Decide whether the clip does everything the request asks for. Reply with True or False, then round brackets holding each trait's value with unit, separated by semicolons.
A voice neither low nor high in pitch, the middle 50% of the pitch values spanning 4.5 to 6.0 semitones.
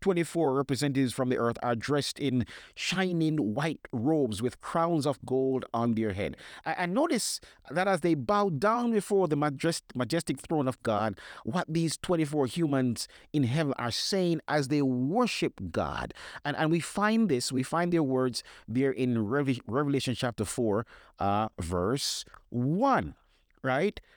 True (145 Hz; 4.9 semitones)